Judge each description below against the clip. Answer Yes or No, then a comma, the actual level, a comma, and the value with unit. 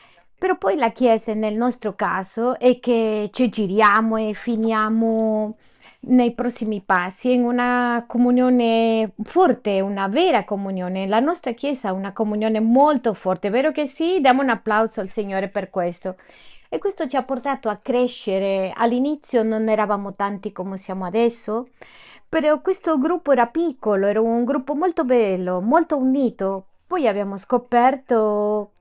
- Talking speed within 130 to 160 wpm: Yes, average, 150 wpm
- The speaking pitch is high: Yes, high, 225 Hz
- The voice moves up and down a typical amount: Yes, average, 3.5 semitones